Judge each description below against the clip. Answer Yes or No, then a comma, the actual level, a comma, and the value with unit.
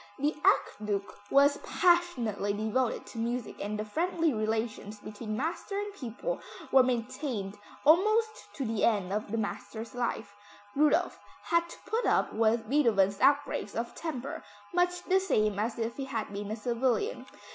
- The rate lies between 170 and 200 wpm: No, average, 155 wpm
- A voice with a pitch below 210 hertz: No, high, 235 Hz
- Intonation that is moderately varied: No, wide, 6.3 semitones